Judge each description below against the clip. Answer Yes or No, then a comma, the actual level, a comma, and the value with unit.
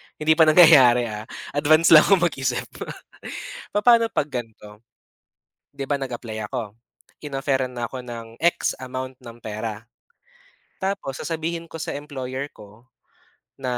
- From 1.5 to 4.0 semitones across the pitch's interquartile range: No, average, 4.7 semitones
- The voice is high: No, low, 130 Hz